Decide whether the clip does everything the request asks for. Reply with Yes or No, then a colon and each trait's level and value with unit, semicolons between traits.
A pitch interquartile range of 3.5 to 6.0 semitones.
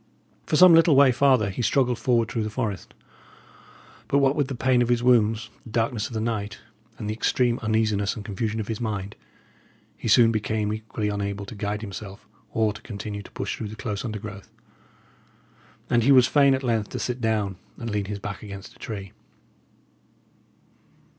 No: average, 2.8 semitones